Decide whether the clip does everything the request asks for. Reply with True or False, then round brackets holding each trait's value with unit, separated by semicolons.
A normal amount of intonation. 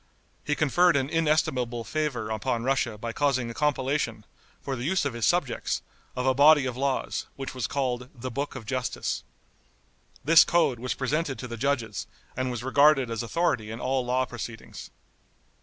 True (3.2 semitones)